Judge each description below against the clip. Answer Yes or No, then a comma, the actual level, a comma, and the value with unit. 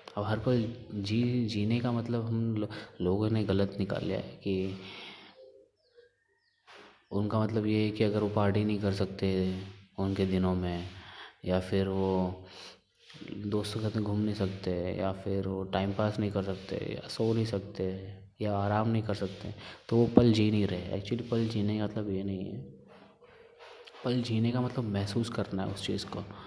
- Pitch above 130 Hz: No, low, 105 Hz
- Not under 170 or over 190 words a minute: Yes, average, 180 wpm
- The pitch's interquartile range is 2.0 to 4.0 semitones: Yes, average, 2.7 semitones